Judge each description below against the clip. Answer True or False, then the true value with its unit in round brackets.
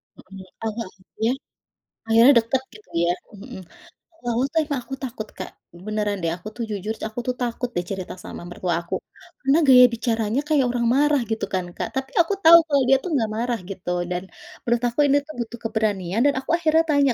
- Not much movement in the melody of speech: False (5.0 semitones)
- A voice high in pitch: True (235 Hz)